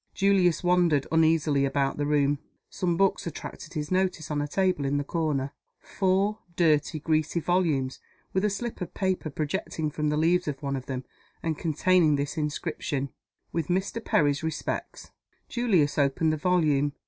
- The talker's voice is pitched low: No, medium, 155 Hz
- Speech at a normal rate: Yes, average, 160 wpm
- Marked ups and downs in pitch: No, average, 3.8 semitones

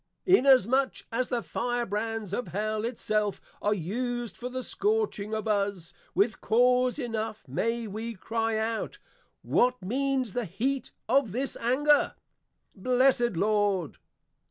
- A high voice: Yes, high, 230 Hz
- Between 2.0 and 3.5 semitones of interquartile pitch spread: Yes, average, 3.2 semitones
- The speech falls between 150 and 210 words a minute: No, slow, 135 wpm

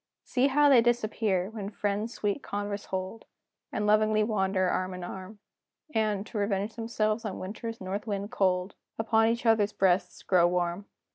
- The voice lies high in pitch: Yes, high, 205 Hz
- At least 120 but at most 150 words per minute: No, average, 160 wpm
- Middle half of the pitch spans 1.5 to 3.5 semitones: Yes, average, 2.7 semitones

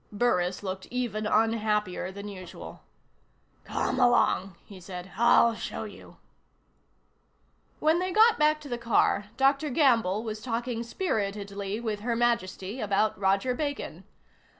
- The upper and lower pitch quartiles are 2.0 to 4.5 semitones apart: Yes, average, 3.8 semitones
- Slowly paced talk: Yes, slow, 125 wpm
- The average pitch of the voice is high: Yes, high, 220 Hz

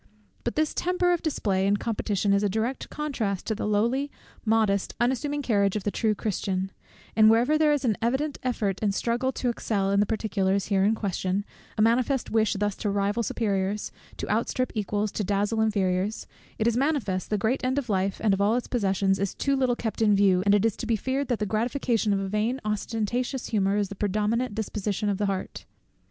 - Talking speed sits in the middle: No, fast, 210 wpm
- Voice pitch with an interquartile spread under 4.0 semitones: Yes, average, 3.2 semitones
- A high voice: Yes, high, 215 Hz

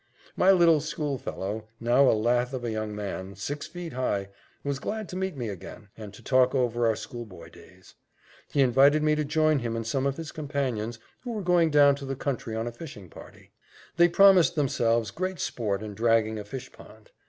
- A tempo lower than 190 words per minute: No, average, 200 wpm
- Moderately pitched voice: No, low, 130 Hz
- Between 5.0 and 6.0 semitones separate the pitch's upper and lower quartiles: Yes, wide, 5.4 semitones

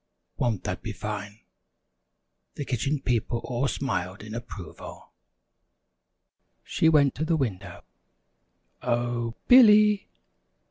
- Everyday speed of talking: No, slow, 105 wpm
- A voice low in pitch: Yes, low, 120 Hz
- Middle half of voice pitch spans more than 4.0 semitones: Yes, average, 4.9 semitones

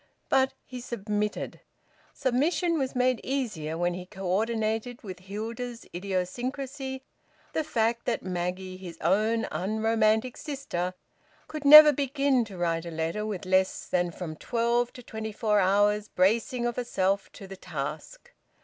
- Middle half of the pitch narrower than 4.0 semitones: No, average, 5.1 semitones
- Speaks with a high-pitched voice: Yes, high, 220 Hz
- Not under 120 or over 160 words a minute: Yes, average, 140 wpm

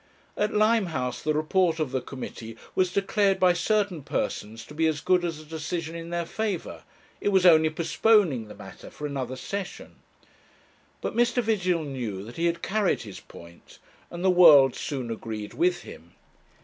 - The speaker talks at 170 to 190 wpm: Yes, average, 175 wpm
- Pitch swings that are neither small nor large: No, wide, 5.9 semitones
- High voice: No, medium, 165 Hz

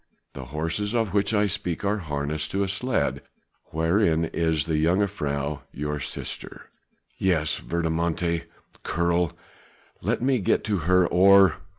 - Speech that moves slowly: Yes, slow, 130 wpm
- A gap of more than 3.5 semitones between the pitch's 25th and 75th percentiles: Yes, average, 3.9 semitones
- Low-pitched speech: Yes, very low, 85 Hz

